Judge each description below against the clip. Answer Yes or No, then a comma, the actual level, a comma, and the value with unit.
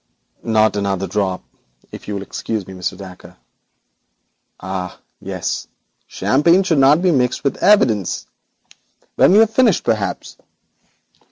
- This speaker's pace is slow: Yes, slow, 125 wpm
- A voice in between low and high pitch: No, low, 110 Hz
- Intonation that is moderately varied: No, wide, 9.0 semitones